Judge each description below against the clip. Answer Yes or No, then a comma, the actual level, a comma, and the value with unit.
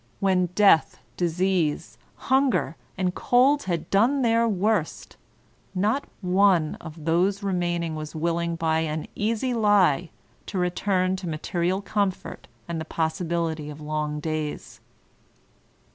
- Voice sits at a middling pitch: Yes, medium, 180 Hz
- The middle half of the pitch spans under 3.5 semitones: No, average, 3.9 semitones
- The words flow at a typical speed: No, slow, 130 wpm